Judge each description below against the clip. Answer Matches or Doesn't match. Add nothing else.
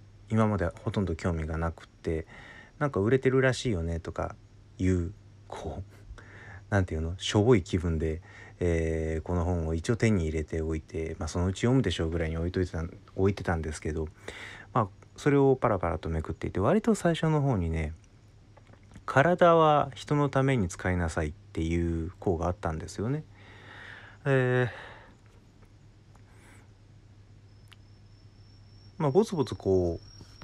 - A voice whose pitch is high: Doesn't match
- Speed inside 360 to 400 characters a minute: Doesn't match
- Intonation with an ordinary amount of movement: Matches